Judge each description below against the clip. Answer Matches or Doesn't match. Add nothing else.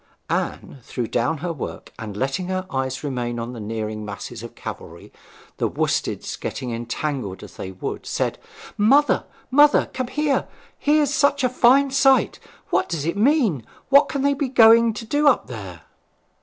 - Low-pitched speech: Doesn't match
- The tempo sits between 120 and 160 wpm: Doesn't match